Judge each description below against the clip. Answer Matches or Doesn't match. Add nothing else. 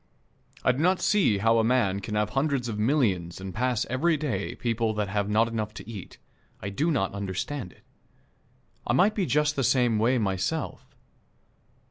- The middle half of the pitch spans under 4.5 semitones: Doesn't match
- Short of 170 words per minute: Doesn't match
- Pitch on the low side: Matches